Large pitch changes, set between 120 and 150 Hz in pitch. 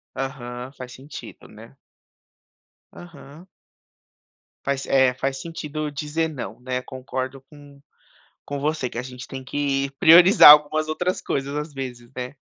No: narrow, 2.6 semitones; medium, 140 Hz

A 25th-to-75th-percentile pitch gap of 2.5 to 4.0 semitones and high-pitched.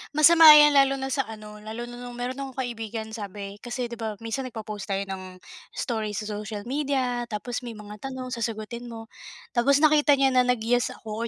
Yes: average, 3.4 semitones; high, 235 Hz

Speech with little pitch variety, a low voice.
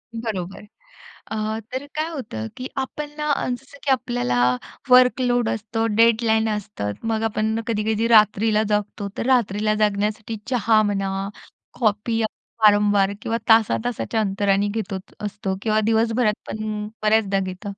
No: narrow, 1.9 semitones; high, 215 Hz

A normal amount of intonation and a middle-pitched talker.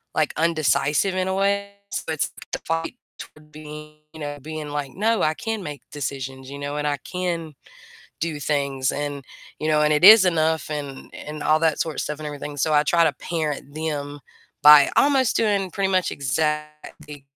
No: narrow, 2.3 semitones; medium, 150 Hz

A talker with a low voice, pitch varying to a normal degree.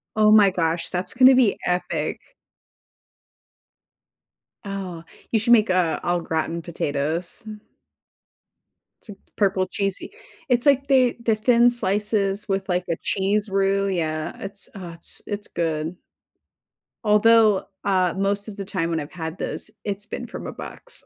No: high, 195 Hz; average, 3.4 semitones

